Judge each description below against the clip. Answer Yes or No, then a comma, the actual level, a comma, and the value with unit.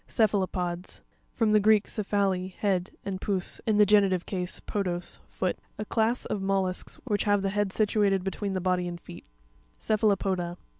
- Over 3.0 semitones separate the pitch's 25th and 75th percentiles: No, narrow, 2.4 semitones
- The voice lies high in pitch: Yes, high, 195 Hz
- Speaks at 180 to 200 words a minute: Yes, average, 195 wpm